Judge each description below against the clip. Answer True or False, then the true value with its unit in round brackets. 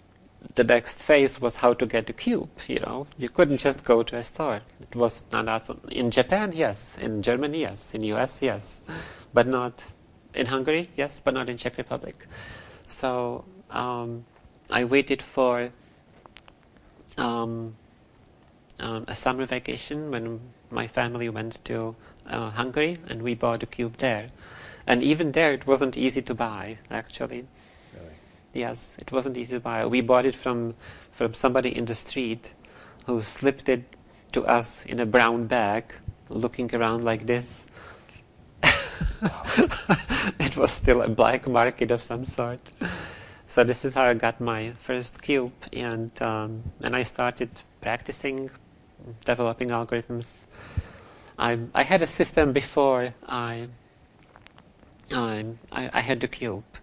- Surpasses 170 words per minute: False (145 wpm)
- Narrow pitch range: True (2.2 semitones)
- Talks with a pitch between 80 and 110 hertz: False (120 Hz)